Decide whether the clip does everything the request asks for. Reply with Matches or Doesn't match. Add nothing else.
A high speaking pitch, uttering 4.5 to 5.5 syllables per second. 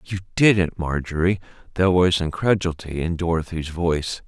Doesn't match